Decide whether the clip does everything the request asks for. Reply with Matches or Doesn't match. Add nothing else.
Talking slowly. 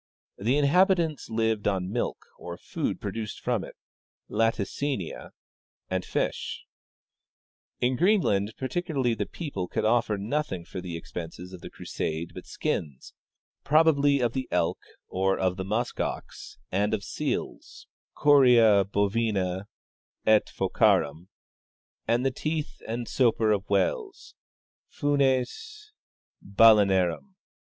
Matches